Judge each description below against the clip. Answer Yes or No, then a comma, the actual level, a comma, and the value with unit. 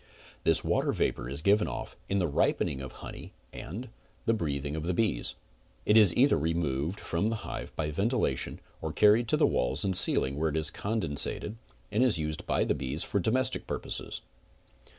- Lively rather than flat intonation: Yes, wide, 6.7 semitones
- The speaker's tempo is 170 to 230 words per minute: Yes, average, 180 wpm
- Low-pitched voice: Yes, very low, 85 Hz